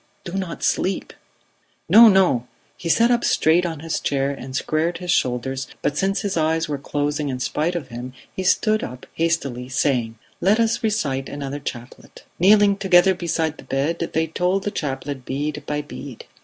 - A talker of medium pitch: Yes, medium, 155 Hz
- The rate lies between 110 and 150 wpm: No, average, 175 wpm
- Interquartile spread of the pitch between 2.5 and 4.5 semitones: No, average, 5.2 semitones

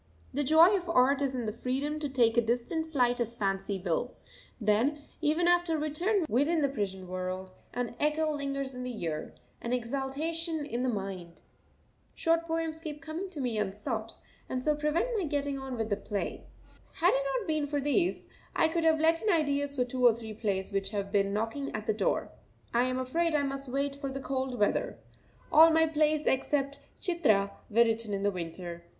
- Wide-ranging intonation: Yes, wide, 5.7 semitones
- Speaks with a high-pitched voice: Yes, very high, 270 Hz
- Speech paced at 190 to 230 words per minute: Yes, average, 195 wpm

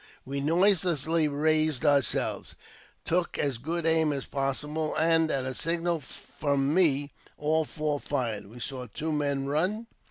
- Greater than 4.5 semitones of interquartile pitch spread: No, average, 2.8 semitones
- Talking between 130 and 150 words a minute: Yes, average, 145 wpm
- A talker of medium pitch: Yes, medium, 150 Hz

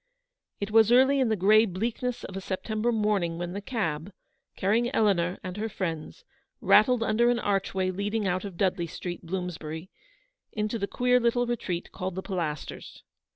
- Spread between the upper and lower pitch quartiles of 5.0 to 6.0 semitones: No, average, 3.8 semitones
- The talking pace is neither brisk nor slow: Yes, average, 170 wpm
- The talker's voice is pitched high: Yes, high, 200 Hz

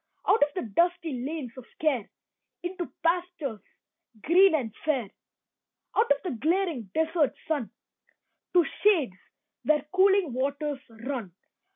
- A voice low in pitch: No, very high, 305 Hz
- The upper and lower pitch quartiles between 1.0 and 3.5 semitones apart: No, wide, 5.5 semitones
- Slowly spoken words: Yes, slow, 125 wpm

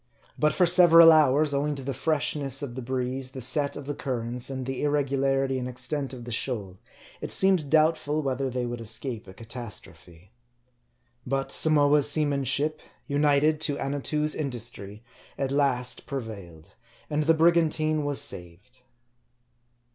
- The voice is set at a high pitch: No, low, 135 Hz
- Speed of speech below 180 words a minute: Yes, average, 155 wpm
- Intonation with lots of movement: No, average, 3.3 semitones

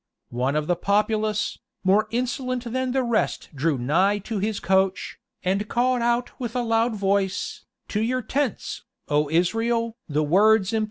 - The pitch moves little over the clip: No, average, 3.9 semitones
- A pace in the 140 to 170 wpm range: Yes, average, 145 wpm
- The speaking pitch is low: No, high, 215 Hz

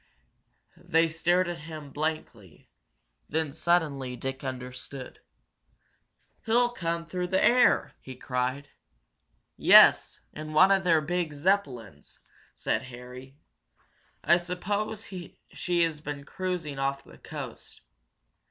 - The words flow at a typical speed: No, slow, 110 wpm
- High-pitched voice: No, medium, 155 Hz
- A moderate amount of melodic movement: Yes, average, 4.7 semitones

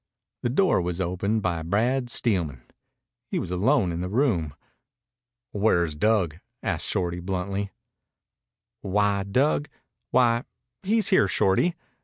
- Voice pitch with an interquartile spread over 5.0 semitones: Yes, wide, 5.5 semitones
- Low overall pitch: Yes, low, 100 Hz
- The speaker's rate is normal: No, slow, 120 wpm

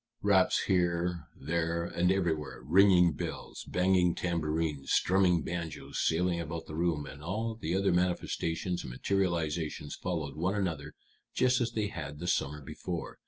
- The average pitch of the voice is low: Yes, very low, 85 Hz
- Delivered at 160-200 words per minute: No, average, 145 wpm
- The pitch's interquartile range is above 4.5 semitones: No, average, 2.8 semitones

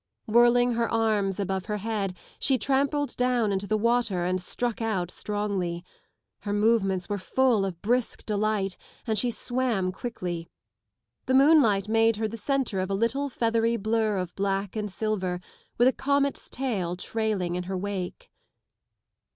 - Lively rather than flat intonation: No, average, 3.7 semitones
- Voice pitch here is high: Yes, high, 215 Hz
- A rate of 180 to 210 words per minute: No, average, 155 wpm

